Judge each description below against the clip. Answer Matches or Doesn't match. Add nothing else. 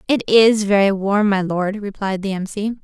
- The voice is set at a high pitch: Matches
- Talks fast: Matches